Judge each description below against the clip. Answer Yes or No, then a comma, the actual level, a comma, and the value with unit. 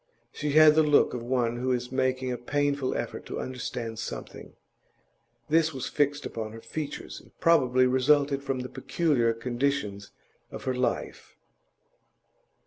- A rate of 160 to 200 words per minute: No, average, 145 wpm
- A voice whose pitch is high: No, low, 130 Hz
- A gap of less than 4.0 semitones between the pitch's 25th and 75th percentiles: Yes, average, 2.9 semitones